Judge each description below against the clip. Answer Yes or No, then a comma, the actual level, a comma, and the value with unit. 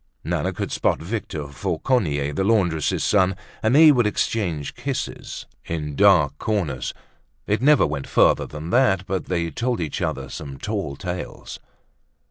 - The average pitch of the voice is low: Yes, very low, 90 Hz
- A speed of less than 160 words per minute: Yes, average, 145 wpm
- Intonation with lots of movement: Yes, wide, 6.6 semitones